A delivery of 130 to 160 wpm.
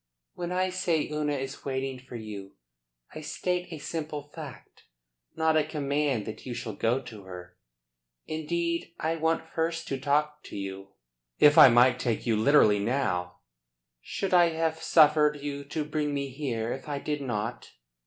No: average, 170 wpm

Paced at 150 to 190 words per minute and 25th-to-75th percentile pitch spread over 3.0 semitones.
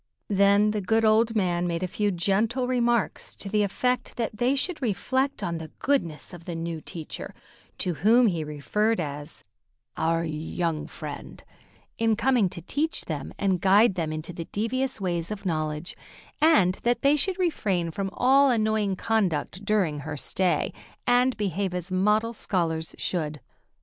Yes: average, 160 wpm; average, 5.3 semitones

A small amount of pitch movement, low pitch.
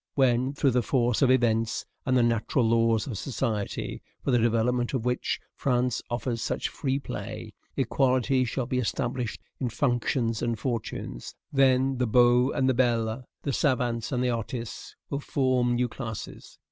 Yes: narrow, 2.0 semitones; low, 125 Hz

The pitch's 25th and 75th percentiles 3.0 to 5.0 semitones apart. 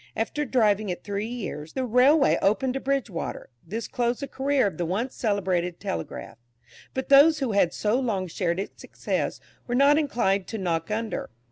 No: wide, 5.6 semitones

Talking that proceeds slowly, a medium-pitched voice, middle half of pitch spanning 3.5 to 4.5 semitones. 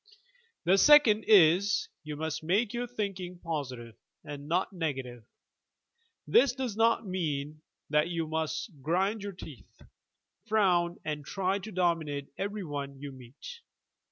No: slow, 130 wpm; medium, 175 Hz; average, 5.2 semitones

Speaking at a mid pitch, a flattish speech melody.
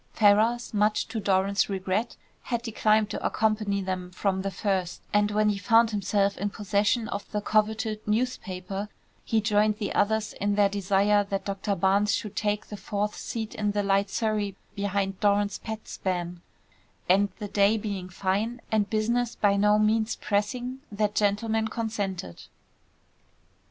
No: high, 205 Hz; narrow, 1.5 semitones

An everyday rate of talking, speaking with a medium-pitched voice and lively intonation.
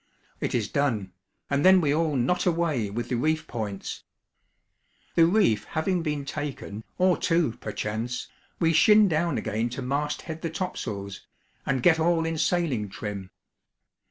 Yes: average, 155 wpm; medium, 150 Hz; wide, 6.4 semitones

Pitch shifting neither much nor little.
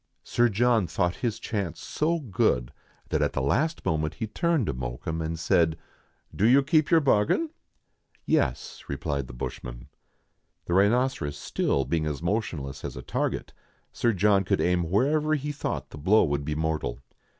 No: wide, 8.3 semitones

